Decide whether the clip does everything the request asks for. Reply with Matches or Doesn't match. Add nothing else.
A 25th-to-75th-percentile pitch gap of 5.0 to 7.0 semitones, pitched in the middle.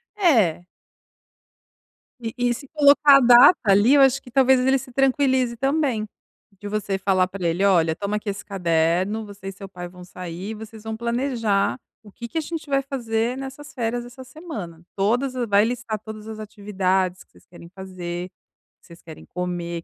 Doesn't match